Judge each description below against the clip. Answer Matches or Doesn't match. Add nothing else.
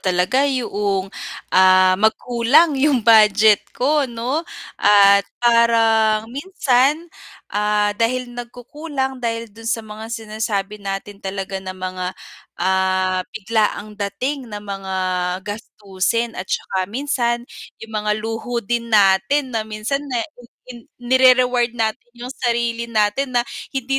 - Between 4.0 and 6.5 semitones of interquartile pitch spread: Doesn't match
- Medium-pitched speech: Doesn't match